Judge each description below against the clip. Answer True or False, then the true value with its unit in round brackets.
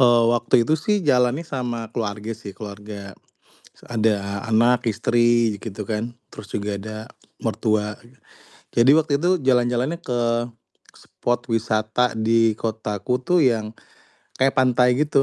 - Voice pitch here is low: True (115 Hz)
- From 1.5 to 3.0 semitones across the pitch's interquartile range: True (2.5 semitones)